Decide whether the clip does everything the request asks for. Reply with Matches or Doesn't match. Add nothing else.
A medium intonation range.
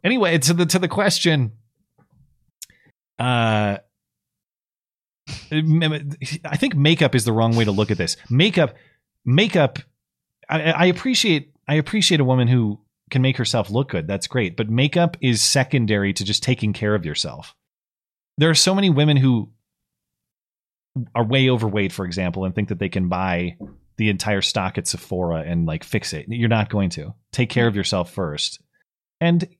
Doesn't match